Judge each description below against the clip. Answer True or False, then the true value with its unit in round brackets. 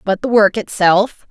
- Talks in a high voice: True (205 Hz)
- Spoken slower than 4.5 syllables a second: True (4.2 syllables/s)